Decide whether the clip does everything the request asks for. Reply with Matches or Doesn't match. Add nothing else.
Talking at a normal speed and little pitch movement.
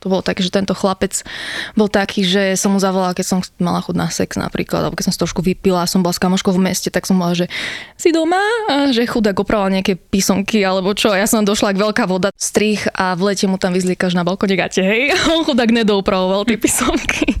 Doesn't match